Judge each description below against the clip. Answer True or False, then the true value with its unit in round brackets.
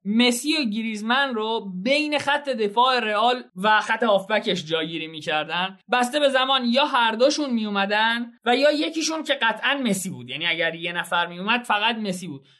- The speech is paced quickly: True (165 wpm)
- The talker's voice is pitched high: True (225 Hz)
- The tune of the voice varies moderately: False (5.7 semitones)